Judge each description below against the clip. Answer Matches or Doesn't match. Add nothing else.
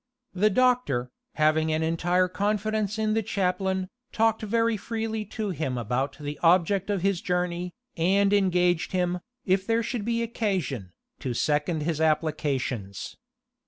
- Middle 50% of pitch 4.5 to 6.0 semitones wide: Matches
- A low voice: Doesn't match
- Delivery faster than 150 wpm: Doesn't match